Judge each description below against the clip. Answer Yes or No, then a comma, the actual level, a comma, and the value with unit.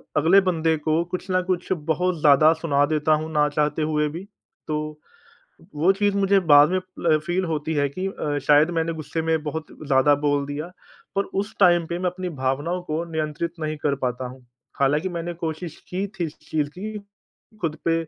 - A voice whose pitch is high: No, medium, 160 Hz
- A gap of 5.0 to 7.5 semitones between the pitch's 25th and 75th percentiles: No, average, 3.0 semitones